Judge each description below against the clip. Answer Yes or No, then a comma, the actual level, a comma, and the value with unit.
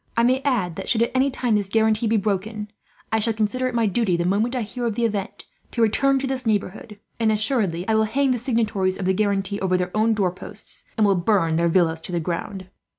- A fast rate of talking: Yes, fast, 245 wpm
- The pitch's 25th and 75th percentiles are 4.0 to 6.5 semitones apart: No, average, 3.6 semitones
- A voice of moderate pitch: No, high, 215 Hz